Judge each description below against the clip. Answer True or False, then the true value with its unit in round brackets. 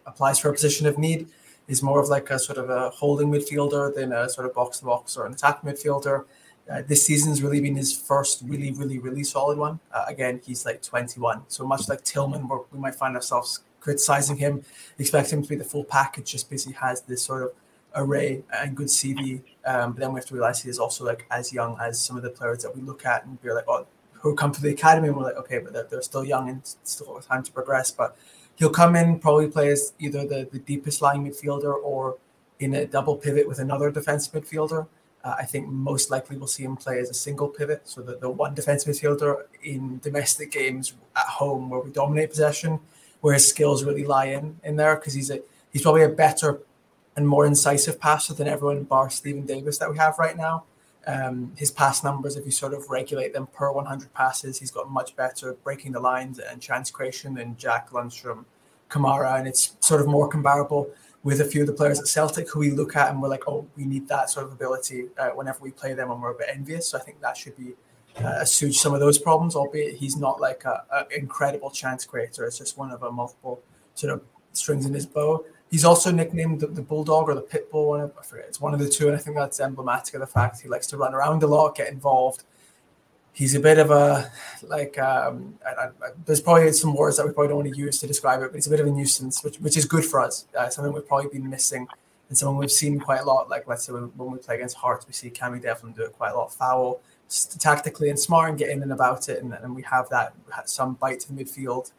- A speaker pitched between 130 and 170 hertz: True (140 Hz)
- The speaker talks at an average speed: False (240 wpm)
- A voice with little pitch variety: True (2.0 semitones)